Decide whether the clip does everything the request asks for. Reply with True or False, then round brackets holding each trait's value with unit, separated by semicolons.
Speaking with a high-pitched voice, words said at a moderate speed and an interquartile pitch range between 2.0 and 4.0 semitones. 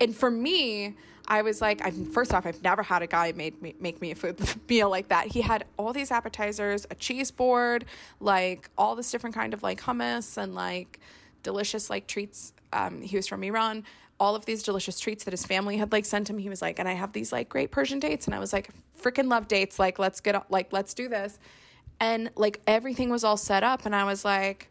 False (205 Hz; 240 wpm; 3.3 semitones)